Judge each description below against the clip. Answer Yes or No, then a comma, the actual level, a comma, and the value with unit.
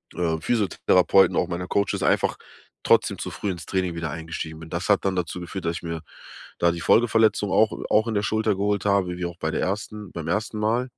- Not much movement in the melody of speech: No, average, 3.7 semitones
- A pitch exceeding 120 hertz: No, very low, 95 Hz